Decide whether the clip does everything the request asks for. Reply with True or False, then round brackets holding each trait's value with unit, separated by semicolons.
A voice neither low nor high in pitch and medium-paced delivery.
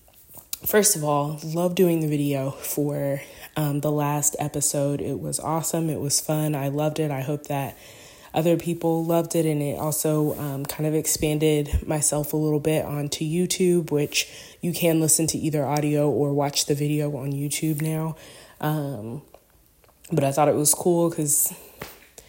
True (150 Hz; 170 wpm)